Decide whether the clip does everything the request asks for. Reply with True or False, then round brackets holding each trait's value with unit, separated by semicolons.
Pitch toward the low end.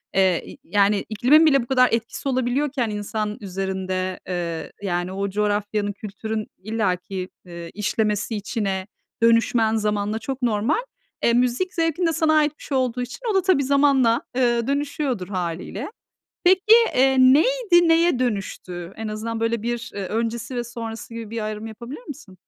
False (225 Hz)